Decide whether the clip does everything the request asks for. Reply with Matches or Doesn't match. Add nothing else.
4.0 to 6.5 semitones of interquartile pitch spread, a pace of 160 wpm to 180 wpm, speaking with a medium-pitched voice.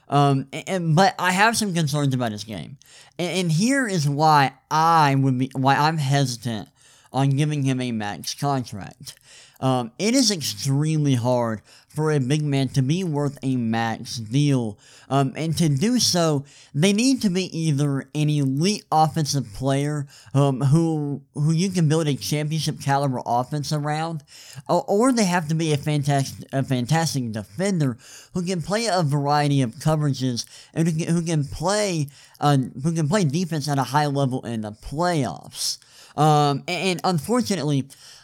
Doesn't match